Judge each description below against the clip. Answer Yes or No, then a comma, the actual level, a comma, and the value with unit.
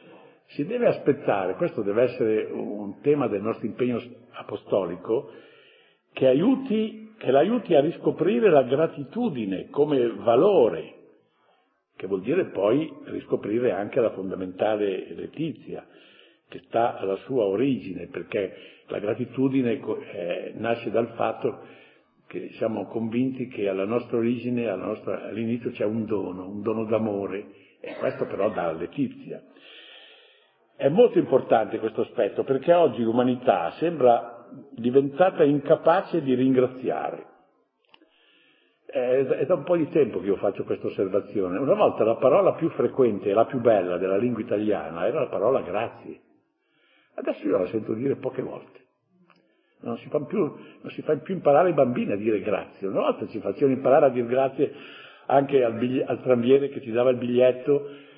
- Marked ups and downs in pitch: Yes, wide, 7.1 semitones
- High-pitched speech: No, low, 130 Hz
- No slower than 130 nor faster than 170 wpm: Yes, average, 145 wpm